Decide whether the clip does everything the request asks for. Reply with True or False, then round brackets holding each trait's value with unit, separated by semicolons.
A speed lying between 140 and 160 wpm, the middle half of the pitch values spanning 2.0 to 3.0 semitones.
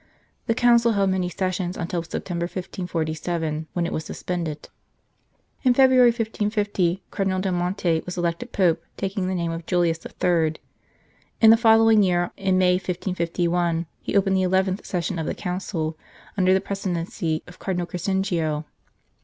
True (155 wpm; 2.4 semitones)